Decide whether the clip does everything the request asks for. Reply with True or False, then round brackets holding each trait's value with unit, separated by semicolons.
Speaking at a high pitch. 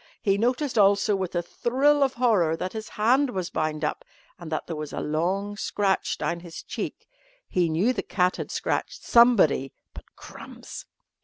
True (195 Hz)